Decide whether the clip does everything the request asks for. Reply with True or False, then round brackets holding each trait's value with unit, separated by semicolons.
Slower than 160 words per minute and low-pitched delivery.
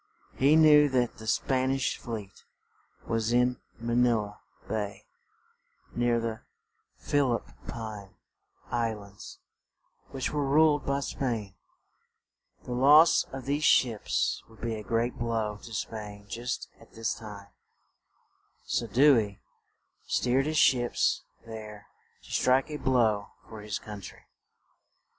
True (135 wpm; 115 Hz)